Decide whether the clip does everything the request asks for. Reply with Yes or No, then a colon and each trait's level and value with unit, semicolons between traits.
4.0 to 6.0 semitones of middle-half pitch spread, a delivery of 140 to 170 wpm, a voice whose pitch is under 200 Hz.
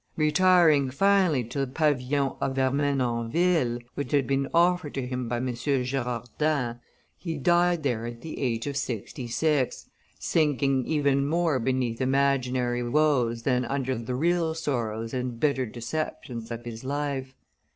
No: average, 3.5 semitones; average, 145 wpm; low, 135 Hz